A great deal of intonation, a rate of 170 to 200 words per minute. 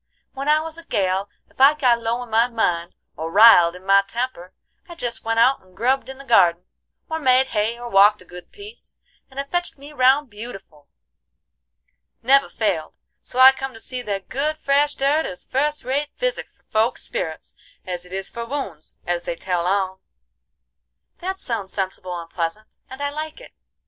Yes: wide, 6.5 semitones; average, 190 wpm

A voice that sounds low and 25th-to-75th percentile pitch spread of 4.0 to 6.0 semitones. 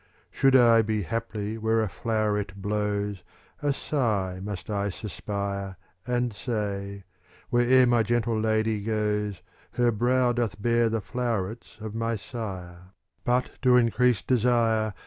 No: low, 110 Hz; average, 2.7 semitones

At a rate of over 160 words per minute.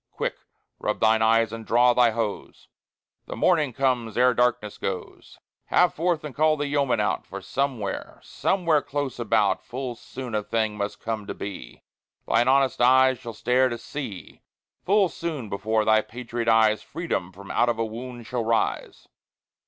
Yes: average, 170 wpm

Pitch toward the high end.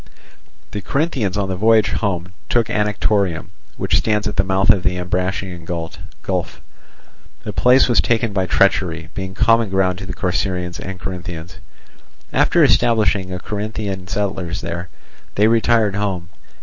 No: very low, 95 Hz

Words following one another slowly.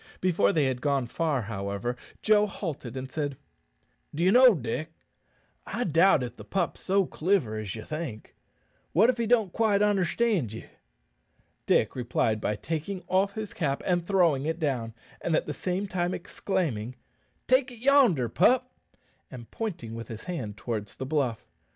No: average, 160 wpm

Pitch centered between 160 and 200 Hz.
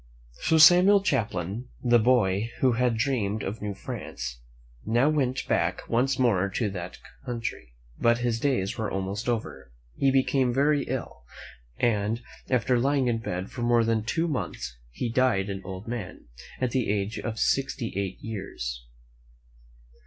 No: low, 115 Hz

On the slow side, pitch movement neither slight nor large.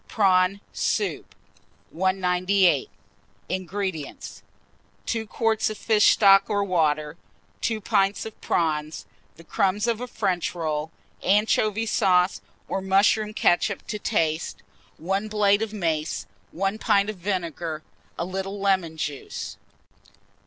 Yes: slow, 115 wpm; average, 3.5 semitones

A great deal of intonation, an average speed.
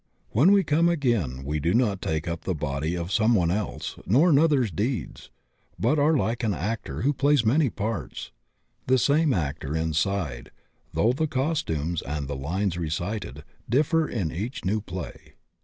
Yes: wide, 8.6 semitones; average, 170 wpm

